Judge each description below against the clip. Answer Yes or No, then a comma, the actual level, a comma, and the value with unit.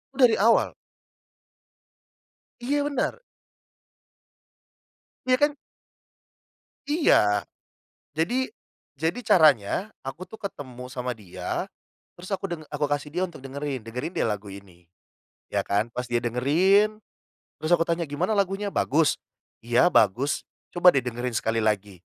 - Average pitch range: No, wide, 8.2 semitones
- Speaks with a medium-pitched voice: Yes, medium, 145 Hz